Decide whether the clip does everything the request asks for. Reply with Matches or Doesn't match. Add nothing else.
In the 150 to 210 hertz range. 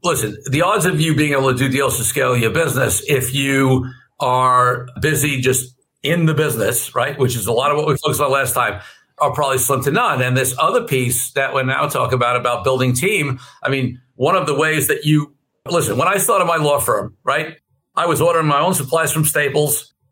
Doesn't match